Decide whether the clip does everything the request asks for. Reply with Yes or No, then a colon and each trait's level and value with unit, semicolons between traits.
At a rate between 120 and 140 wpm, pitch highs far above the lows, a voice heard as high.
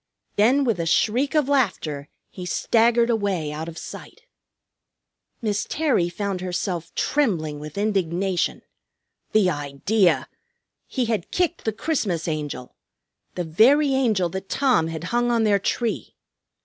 Yes: slow, 135 wpm; wide, 6.2 semitones; high, 200 Hz